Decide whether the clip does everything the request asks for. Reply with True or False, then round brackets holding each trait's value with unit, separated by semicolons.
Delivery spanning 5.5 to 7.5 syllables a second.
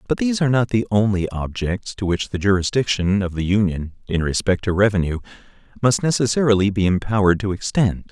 True (6.1 syllables/s)